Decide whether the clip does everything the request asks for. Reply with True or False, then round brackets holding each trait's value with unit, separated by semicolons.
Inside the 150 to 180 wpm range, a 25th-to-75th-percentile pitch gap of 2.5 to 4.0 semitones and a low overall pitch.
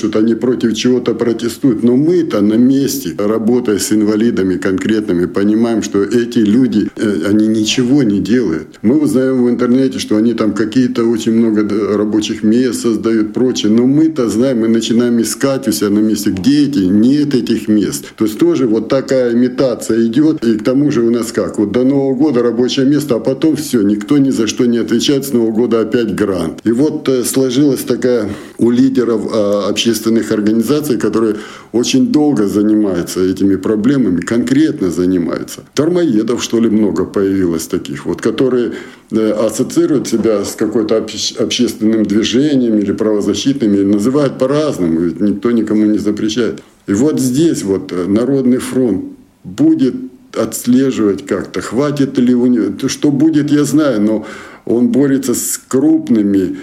True (155 wpm; 3.4 semitones; 115 Hz)